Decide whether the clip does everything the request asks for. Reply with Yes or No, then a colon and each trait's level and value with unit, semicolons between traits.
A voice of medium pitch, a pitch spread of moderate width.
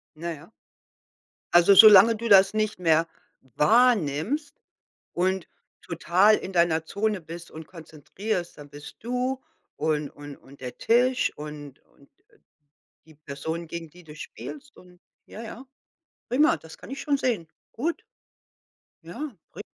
No: medium, 175 Hz; wide, 6.1 semitones